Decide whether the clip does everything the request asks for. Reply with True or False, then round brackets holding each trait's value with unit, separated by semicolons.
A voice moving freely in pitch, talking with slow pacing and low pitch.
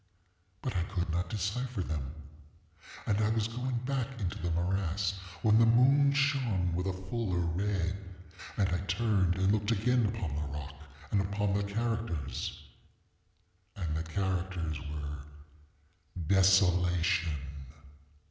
False (4.2 semitones; 130 wpm; 95 Hz)